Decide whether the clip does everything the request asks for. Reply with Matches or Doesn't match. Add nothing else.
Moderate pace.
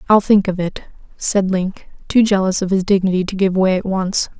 Doesn't match